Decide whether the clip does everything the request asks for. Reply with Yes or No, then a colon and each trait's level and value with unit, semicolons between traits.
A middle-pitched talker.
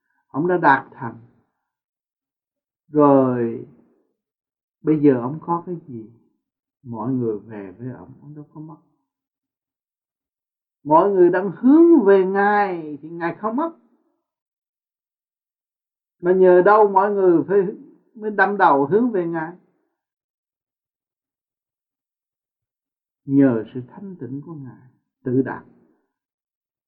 Yes: medium, 170 Hz